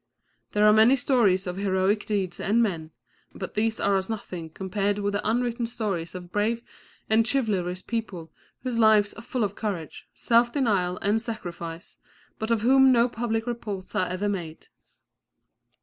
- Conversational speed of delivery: Yes, average, 165 wpm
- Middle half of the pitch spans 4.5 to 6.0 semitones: No, average, 3.5 semitones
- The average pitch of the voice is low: No, high, 210 Hz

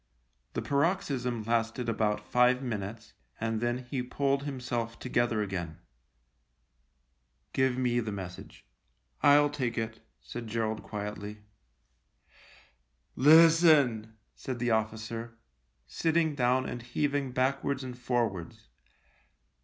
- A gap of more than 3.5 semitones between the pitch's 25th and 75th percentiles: No, average, 3.2 semitones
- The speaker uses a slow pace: Yes, slow, 110 wpm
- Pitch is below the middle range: Yes, low, 120 Hz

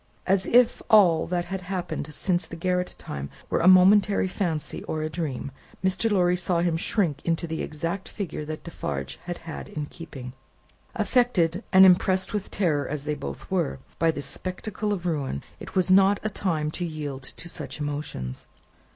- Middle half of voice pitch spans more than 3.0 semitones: Yes, average, 3.7 semitones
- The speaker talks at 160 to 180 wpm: Yes, average, 175 wpm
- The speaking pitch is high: No, medium, 175 Hz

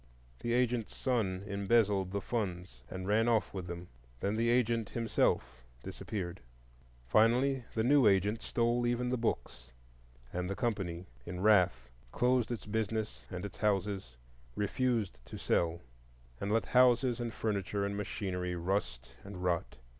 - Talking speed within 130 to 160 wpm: Yes, average, 145 wpm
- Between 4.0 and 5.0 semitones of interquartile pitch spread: Yes, average, 4.3 semitones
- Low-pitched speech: Yes, low, 105 Hz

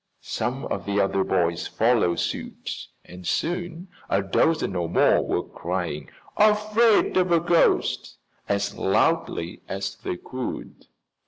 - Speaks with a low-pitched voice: Yes, low, 100 Hz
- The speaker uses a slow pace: Yes, slow, 130 wpm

